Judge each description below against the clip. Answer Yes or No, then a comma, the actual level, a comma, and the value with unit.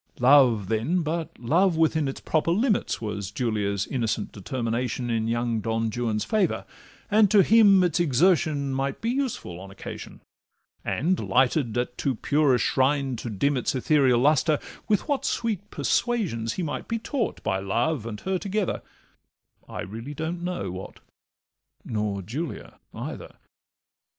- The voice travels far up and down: Yes, wide, 7.3 semitones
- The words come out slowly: No, average, 150 wpm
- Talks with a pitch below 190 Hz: Yes, low, 135 Hz